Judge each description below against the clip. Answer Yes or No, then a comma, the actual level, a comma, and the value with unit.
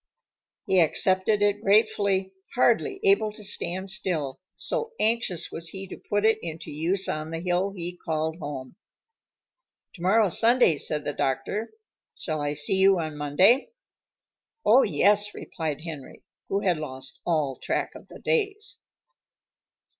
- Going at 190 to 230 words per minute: No, average, 140 wpm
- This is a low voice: No, medium, 185 Hz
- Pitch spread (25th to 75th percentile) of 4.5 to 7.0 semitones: Yes, average, 5.0 semitones